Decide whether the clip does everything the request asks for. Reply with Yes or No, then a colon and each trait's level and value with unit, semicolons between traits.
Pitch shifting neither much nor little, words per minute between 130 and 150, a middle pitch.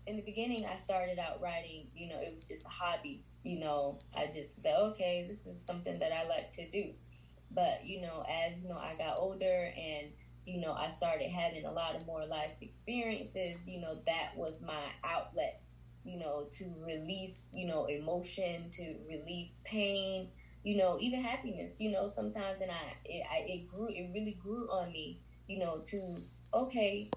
No: average, 4.2 semitones; average, 190 wpm; medium, 175 Hz